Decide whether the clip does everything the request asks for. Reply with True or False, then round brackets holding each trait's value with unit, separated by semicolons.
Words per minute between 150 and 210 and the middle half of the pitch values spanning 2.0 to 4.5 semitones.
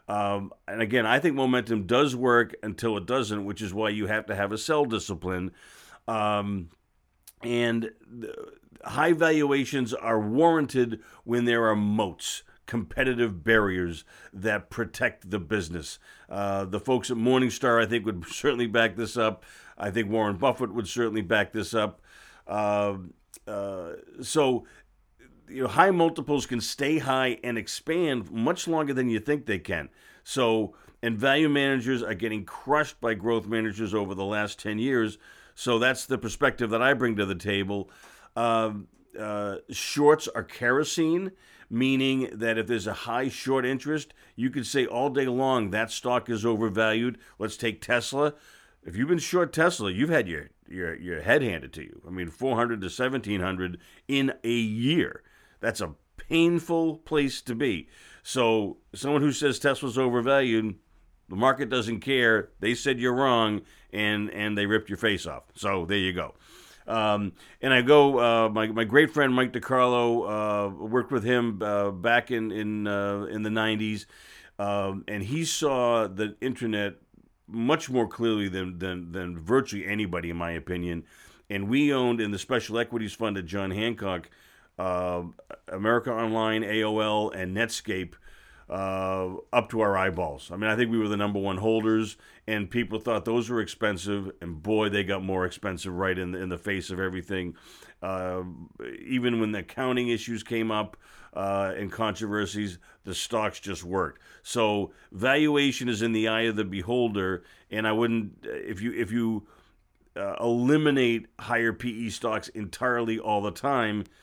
True (165 wpm; 3.5 semitones)